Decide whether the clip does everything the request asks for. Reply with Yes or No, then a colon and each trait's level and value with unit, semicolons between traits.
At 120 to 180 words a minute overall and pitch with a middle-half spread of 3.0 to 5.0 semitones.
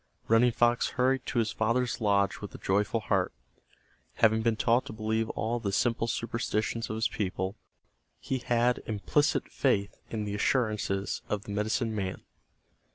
No: average, 160 wpm; narrow, 2.4 semitones